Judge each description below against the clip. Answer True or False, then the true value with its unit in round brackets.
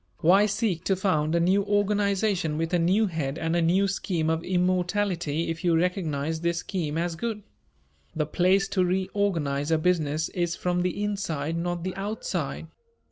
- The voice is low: False (175 Hz)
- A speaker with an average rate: True (170 wpm)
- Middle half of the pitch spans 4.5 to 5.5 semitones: False (3.1 semitones)